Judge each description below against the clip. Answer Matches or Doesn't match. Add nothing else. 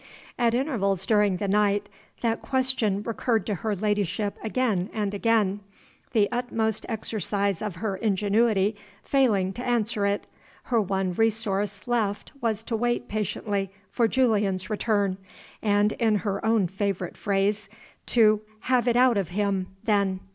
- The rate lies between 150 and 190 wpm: Doesn't match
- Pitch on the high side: Matches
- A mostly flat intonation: Matches